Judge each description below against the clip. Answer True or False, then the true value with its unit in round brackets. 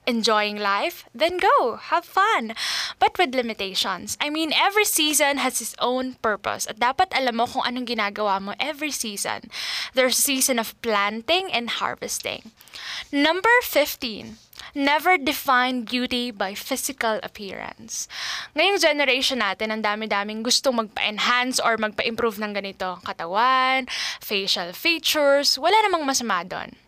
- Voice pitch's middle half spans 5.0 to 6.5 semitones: True (5.6 semitones)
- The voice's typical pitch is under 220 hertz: False (250 Hz)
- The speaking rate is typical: True (135 wpm)